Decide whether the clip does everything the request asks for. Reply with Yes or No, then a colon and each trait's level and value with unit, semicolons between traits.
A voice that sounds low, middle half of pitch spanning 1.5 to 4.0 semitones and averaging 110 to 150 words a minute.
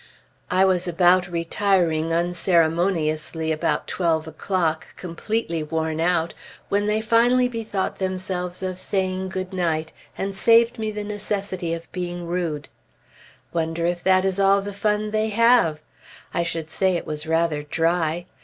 No: medium, 180 Hz; average, 3.1 semitones; average, 145 wpm